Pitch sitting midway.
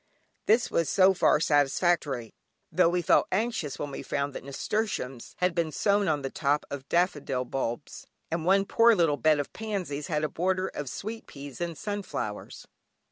Yes: medium, 160 Hz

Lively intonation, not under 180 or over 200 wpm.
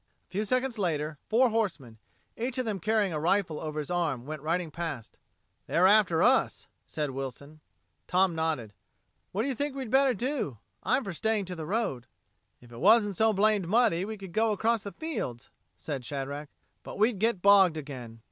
Yes: wide, 6.5 semitones; average, 185 wpm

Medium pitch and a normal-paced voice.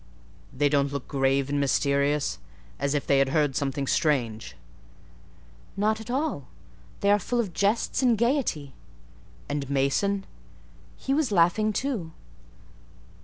No: medium, 150 Hz; slow, 130 wpm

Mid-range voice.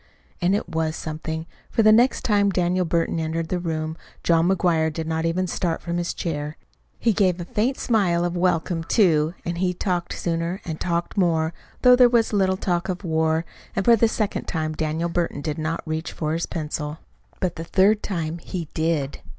Yes: medium, 170 Hz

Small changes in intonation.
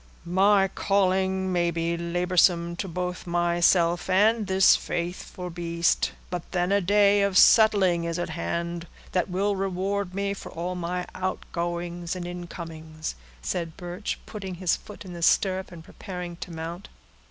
Yes: narrow, 1.9 semitones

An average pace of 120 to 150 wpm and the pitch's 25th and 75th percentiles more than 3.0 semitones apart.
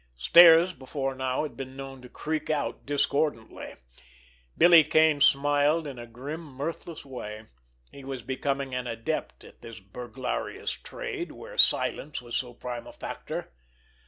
Yes: average, 145 wpm; average, 3.7 semitones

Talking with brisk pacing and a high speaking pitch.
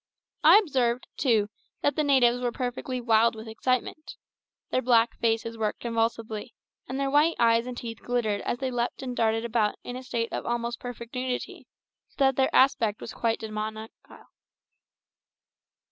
No: average, 160 wpm; high, 235 Hz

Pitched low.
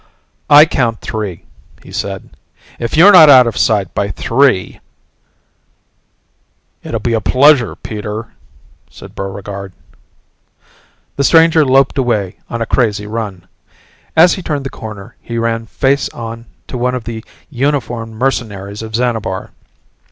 Yes: low, 115 Hz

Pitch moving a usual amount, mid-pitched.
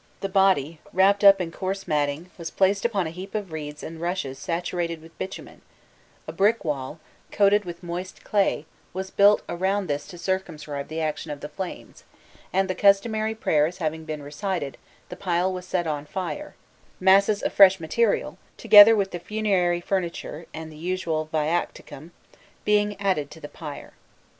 Yes: average, 3.7 semitones; medium, 180 Hz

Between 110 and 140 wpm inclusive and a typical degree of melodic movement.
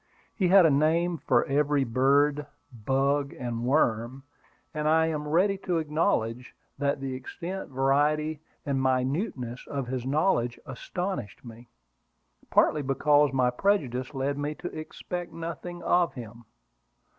Yes: slow, 135 wpm; average, 3.7 semitones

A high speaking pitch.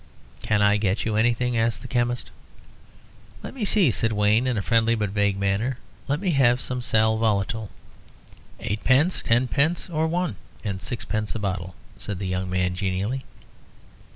No: low, 110 Hz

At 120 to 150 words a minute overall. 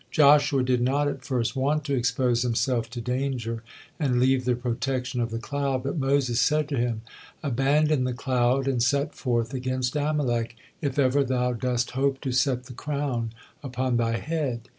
No: average, 175 wpm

